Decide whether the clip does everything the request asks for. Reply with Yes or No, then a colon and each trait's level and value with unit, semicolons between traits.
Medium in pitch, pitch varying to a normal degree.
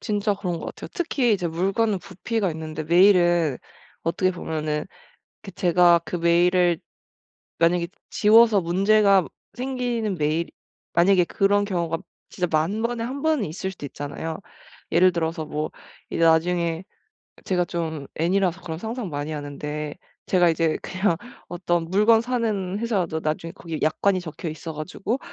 Yes: medium, 180 Hz; average, 3.8 semitones